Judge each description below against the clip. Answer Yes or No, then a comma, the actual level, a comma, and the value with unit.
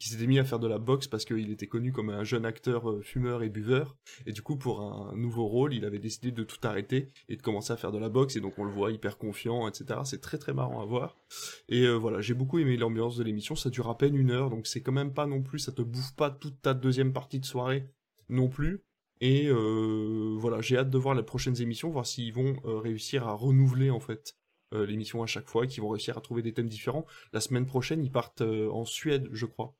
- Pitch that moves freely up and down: No, average, 3.0 semitones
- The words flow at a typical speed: No, fast, 265 wpm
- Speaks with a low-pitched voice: Yes, low, 120 Hz